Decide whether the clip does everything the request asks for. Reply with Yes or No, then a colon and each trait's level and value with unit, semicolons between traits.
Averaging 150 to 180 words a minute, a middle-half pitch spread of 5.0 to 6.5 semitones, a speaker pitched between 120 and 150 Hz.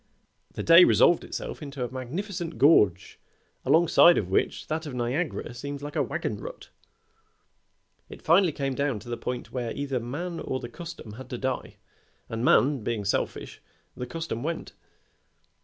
Yes: average, 160 wpm; average, 5.3 semitones; medium, 140 Hz